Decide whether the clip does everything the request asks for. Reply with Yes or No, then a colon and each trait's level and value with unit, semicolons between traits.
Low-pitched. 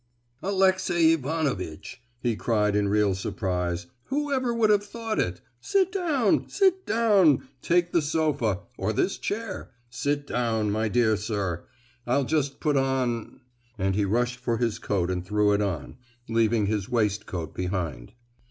Yes: low, 120 Hz